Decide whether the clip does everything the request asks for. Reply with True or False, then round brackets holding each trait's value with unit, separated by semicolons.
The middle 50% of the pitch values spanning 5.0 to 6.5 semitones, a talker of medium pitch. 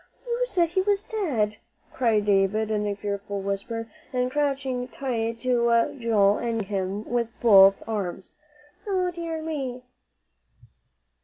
False (5.3 semitones; 230 Hz)